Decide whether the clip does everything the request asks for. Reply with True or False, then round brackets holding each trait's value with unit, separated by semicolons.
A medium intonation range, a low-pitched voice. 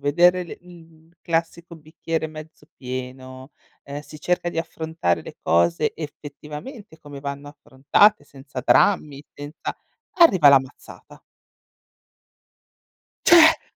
False (3.1 semitones; 150 Hz)